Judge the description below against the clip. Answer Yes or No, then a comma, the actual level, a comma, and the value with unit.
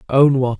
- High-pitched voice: No, low, 130 Hz